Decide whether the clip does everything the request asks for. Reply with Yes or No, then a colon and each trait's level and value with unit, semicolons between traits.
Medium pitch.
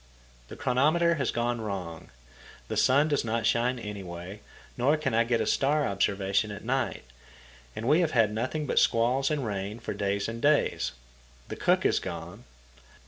No: low, 115 Hz